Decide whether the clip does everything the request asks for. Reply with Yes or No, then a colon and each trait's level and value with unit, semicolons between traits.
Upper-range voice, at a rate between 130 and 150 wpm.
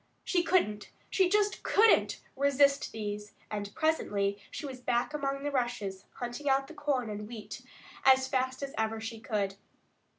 No: very high, 255 Hz; average, 160 wpm